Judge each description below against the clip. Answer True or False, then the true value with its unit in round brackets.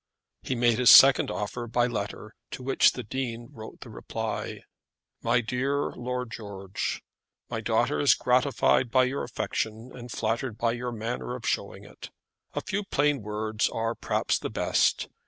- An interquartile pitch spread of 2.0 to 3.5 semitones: True (2.5 semitones)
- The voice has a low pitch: True (120 Hz)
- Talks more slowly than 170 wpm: True (160 wpm)